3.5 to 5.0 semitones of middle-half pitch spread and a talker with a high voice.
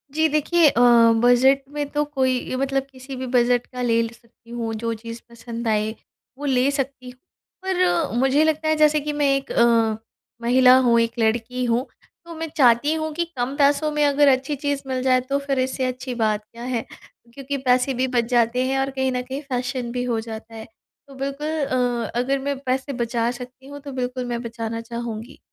No: average, 2.8 semitones; very high, 255 Hz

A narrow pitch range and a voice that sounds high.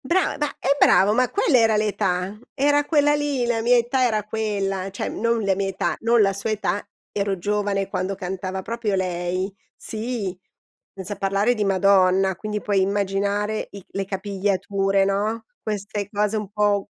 Yes: narrow, 2.3 semitones; high, 205 Hz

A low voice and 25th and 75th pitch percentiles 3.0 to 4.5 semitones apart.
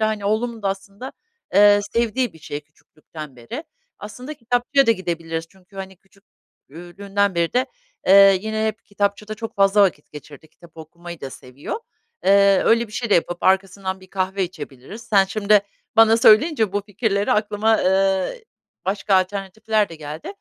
No: high, 200 Hz; average, 3.5 semitones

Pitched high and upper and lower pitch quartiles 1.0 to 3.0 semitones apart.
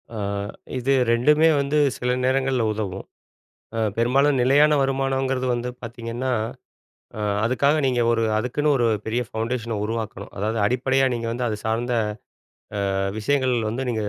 No: low, 125 Hz; average, 2.7 semitones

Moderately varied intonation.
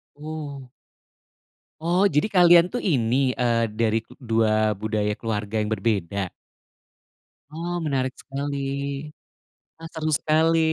No: wide, 6.4 semitones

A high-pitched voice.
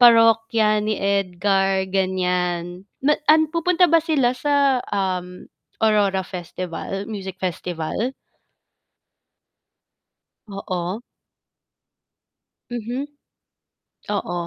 Yes: high, 195 Hz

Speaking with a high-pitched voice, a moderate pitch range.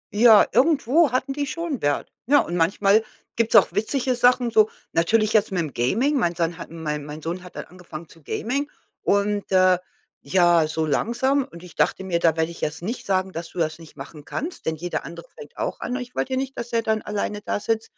No: high, 200 Hz; wide, 6.5 semitones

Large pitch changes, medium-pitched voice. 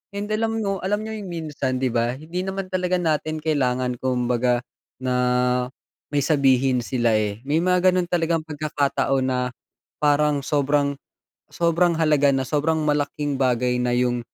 No: average, 4.7 semitones; medium, 145 Hz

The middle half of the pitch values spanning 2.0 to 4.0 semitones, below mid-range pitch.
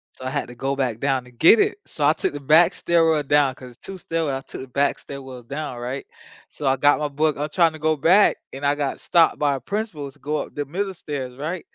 No: average, 2.9 semitones; medium, 145 Hz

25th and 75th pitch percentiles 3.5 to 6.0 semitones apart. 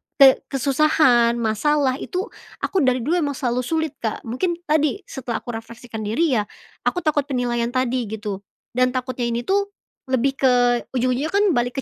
Yes: average, 4.0 semitones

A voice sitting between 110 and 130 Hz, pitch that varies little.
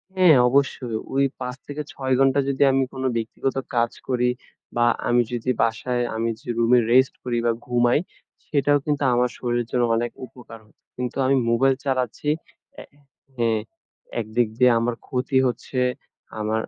Yes: low, 125 Hz; narrow, 2.0 semitones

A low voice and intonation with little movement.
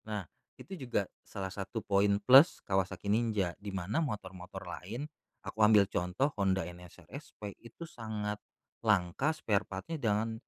No: low, 105 Hz; average, 3.0 semitones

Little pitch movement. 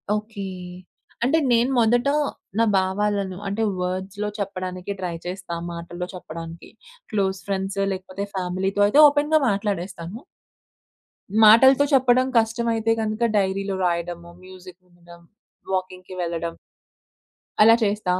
No: average, 3.3 semitones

